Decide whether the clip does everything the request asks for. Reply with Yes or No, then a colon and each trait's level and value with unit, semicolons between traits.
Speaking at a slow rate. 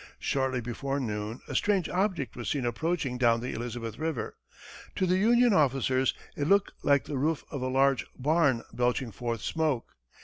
No: average, 170 wpm